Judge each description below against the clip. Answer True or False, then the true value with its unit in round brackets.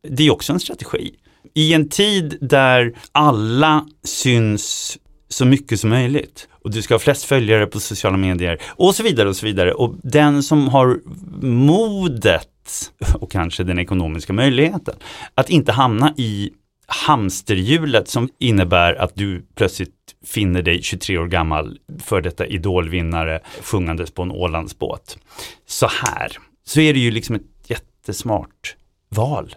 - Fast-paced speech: False (145 wpm)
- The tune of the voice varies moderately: False (7.8 semitones)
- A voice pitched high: False (115 Hz)